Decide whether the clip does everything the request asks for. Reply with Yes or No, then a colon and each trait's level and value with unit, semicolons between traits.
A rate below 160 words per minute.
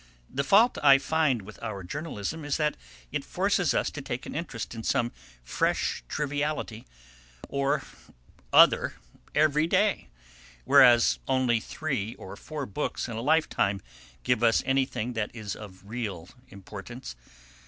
Yes: average, 140 wpm